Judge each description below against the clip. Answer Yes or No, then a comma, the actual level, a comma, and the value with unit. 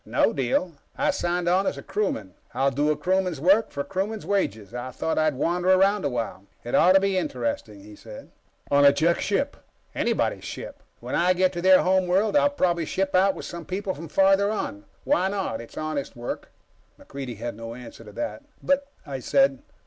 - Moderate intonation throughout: No, wide, 6.2 semitones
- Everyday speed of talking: No, fast, 210 wpm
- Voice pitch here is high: No, medium, 175 Hz